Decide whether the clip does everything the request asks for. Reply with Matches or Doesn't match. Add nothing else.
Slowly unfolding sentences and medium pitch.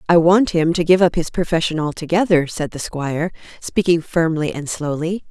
Doesn't match